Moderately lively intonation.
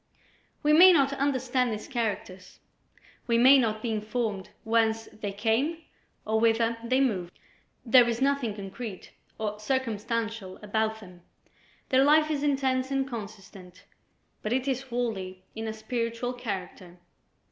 Yes: average, 3.6 semitones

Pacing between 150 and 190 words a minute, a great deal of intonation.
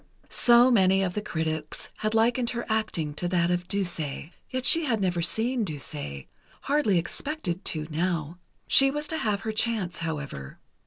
Yes: average, 165 wpm; wide, 6.1 semitones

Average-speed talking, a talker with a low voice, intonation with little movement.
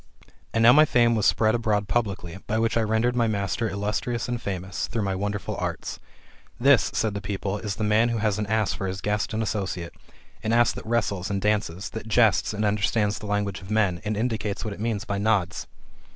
No: fast, 220 wpm; low, 105 Hz; narrow, 2.1 semitones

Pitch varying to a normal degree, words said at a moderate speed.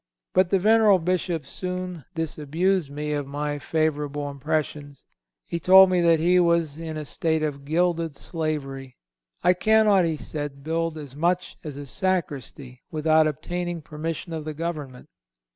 Yes: average, 3.1 semitones; average, 150 wpm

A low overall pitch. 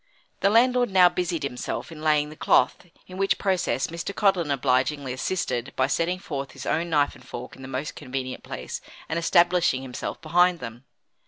No: medium, 155 Hz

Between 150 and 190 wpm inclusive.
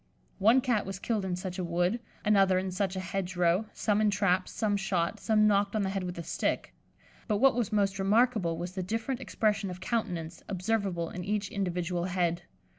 No: average, 200 wpm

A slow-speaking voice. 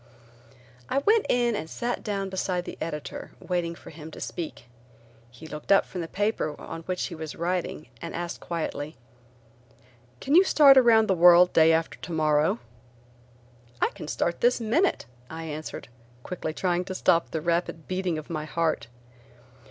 No: average, 165 wpm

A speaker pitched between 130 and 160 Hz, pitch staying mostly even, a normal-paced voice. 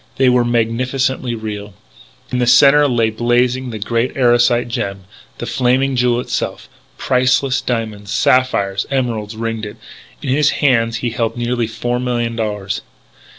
No: low, 120 Hz; narrow, 2.1 semitones; average, 150 wpm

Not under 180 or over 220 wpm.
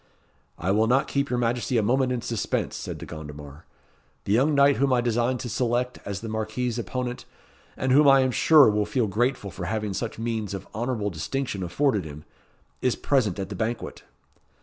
Yes: average, 195 wpm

